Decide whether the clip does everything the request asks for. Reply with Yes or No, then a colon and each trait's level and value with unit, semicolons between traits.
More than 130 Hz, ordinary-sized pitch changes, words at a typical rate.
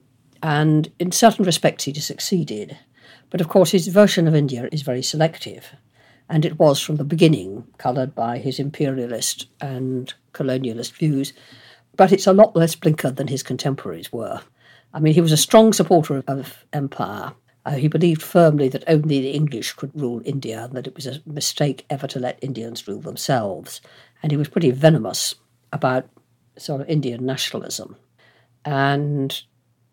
Yes: medium, 140 Hz; average, 3.7 semitones; average, 170 wpm